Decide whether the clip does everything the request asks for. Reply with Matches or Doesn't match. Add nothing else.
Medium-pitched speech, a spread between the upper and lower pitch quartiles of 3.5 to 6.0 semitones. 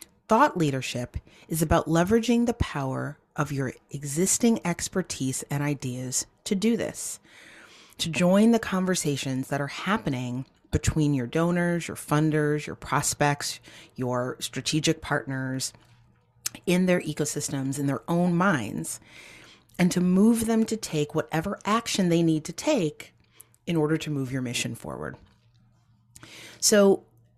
Matches